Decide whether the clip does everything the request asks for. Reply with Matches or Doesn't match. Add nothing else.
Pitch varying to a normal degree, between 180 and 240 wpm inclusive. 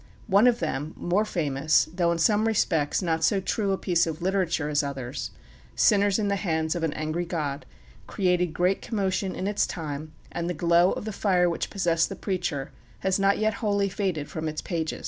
Matches